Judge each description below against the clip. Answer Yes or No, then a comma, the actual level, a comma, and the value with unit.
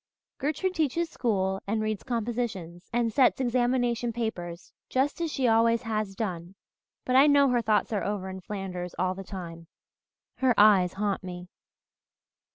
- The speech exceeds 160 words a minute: No, average, 155 wpm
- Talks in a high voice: Yes, high, 215 Hz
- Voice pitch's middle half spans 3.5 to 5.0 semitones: Yes, average, 4.5 semitones